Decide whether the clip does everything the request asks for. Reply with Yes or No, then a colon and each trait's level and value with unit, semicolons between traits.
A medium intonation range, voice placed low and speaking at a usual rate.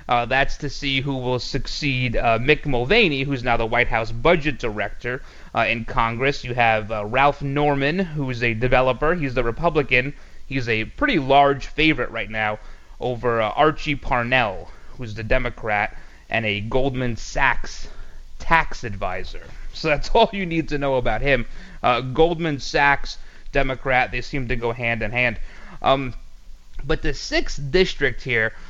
Yes: average, 3.7 semitones; low, 130 Hz; average, 165 wpm